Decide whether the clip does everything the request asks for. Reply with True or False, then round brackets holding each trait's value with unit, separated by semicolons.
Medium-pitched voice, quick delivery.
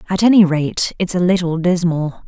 False (175 Hz; 185 wpm)